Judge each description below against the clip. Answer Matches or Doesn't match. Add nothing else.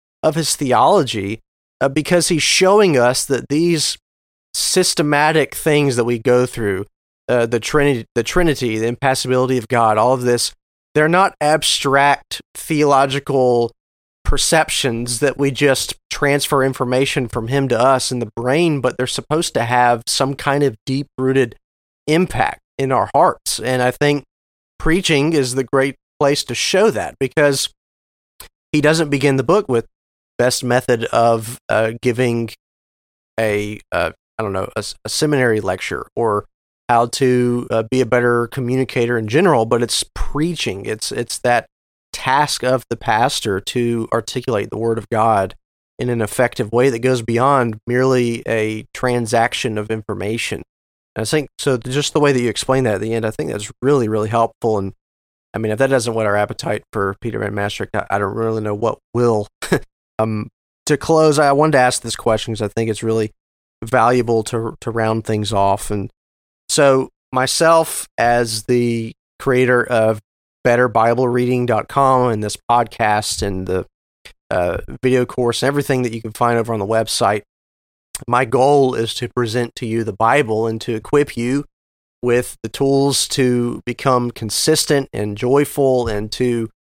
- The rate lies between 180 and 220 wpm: Doesn't match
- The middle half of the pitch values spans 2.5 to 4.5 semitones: Matches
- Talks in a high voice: Doesn't match